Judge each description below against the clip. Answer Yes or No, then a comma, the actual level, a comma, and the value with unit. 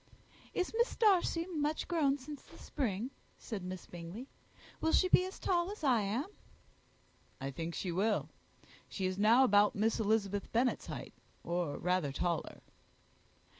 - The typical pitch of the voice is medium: No, high, 225 Hz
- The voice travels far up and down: Yes, wide, 8.5 semitones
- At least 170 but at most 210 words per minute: No, average, 150 wpm